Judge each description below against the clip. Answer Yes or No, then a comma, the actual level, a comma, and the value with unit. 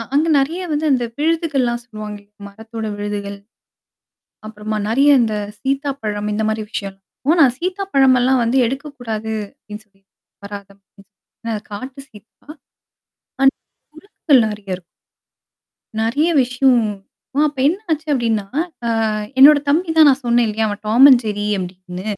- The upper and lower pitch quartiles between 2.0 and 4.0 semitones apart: No, average, 5.0 semitones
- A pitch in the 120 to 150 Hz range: No, high, 240 Hz